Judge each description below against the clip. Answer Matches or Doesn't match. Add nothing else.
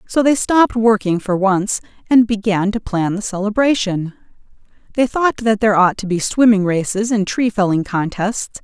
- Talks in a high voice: Matches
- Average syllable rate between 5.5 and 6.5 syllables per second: Doesn't match